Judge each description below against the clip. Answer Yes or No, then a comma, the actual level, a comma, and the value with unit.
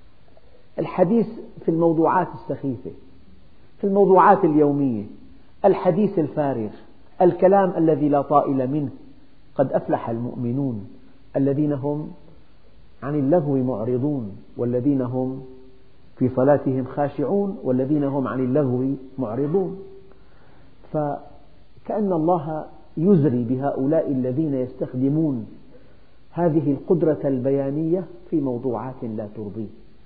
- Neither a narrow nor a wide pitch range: Yes, average, 4.0 semitones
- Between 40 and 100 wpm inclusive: Yes, average, 90 wpm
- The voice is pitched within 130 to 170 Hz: Yes, medium, 140 Hz